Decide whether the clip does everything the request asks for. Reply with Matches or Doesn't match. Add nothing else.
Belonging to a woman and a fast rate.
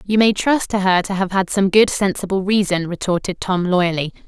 Matches